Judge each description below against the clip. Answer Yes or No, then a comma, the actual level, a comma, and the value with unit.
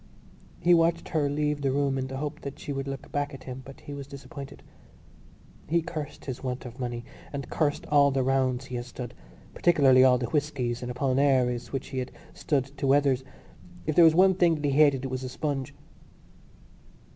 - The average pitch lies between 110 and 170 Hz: Yes, low, 135 Hz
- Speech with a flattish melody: Yes, narrow, 2.2 semitones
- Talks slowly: No, fast, 205 wpm